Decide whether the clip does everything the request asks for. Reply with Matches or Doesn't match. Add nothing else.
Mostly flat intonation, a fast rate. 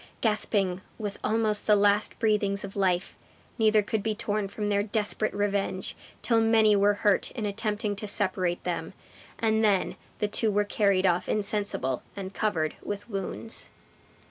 Doesn't match